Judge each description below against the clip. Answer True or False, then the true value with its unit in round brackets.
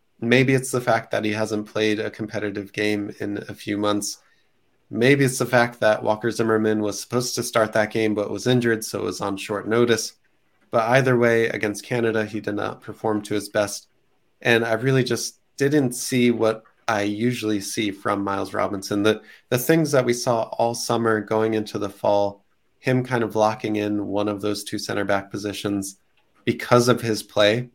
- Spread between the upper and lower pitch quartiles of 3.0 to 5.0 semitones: False (2.5 semitones)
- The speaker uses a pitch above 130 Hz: False (110 Hz)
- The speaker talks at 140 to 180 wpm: False (195 wpm)